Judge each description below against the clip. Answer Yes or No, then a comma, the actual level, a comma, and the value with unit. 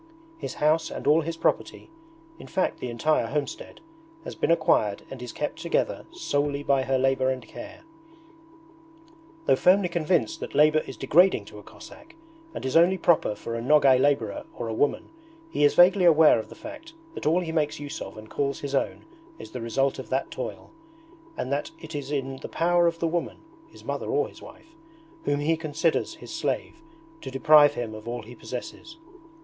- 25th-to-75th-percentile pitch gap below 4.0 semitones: No, average, 4.5 semitones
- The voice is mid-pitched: Yes, medium, 150 Hz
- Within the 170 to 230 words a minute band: Yes, average, 195 wpm